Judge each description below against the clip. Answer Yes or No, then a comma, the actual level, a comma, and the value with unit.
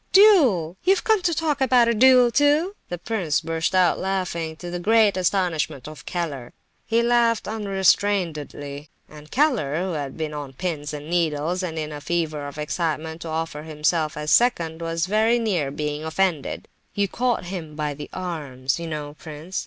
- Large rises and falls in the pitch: Yes, wide, 5.7 semitones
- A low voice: No, medium, 170 Hz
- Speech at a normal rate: Yes, average, 175 wpm